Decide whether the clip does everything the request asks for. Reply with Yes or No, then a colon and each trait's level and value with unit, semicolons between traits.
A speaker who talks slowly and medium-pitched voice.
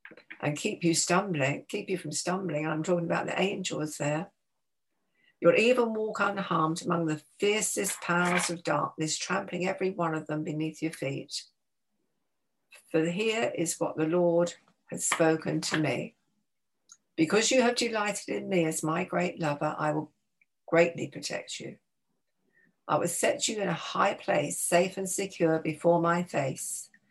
No: average, 155 wpm; medium, 170 Hz